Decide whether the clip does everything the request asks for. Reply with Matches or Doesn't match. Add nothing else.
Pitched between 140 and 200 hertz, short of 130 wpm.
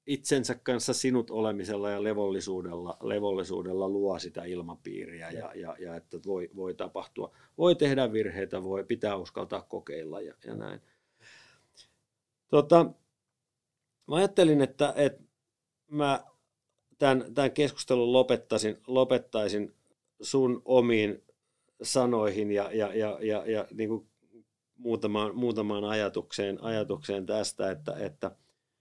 Doesn't match